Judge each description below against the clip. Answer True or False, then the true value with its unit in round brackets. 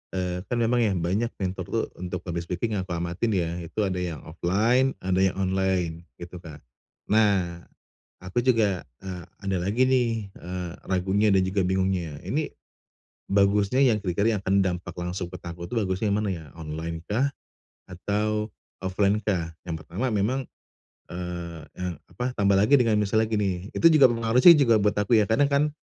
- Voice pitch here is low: True (95 Hz)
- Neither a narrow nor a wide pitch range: True (3.7 semitones)